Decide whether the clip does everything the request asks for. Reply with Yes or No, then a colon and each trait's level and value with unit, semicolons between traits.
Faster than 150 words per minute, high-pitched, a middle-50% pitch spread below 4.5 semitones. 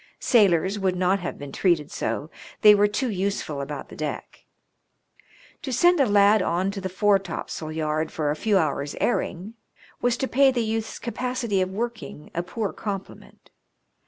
No: average, 165 wpm; high, 195 Hz; average, 4.9 semitones